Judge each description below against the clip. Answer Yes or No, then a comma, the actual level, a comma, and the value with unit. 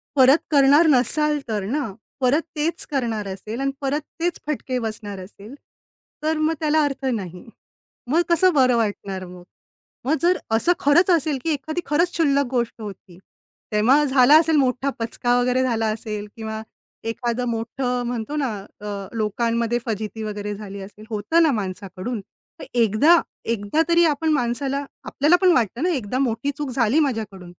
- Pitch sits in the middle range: No, very high, 250 Hz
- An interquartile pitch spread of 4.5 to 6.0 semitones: Yes, wide, 5.4 semitones